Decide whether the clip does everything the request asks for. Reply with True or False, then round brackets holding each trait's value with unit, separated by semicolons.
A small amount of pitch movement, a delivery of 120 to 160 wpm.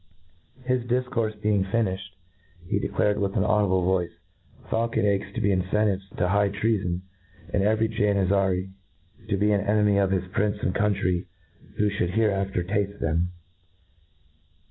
True (2.0 semitones; 155 wpm)